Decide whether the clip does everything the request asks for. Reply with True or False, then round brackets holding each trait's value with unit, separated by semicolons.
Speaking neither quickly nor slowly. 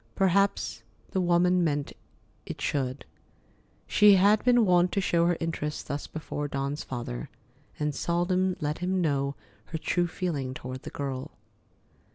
True (145 wpm)